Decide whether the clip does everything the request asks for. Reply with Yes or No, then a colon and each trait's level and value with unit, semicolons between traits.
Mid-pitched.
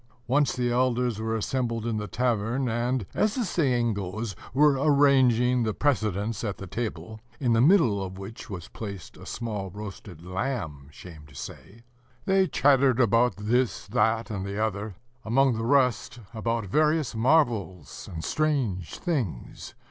No: low, 115 Hz